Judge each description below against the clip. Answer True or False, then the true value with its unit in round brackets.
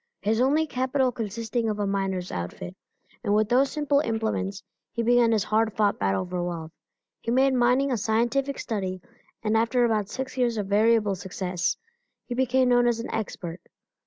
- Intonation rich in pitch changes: False (3.9 semitones)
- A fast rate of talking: False (175 wpm)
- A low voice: False (225 Hz)